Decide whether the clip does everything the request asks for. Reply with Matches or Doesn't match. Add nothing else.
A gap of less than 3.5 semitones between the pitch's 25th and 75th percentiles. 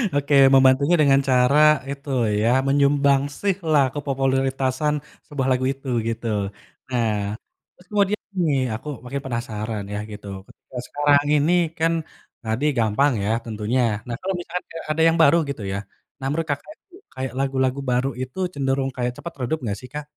Matches